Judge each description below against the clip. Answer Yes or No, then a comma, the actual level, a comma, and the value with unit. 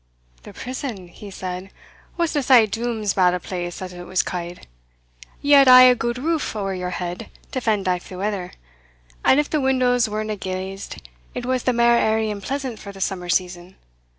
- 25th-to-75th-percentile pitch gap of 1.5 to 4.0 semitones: No, average, 5.2 semitones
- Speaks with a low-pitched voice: No, high, 210 Hz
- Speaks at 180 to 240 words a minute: Yes, average, 190 wpm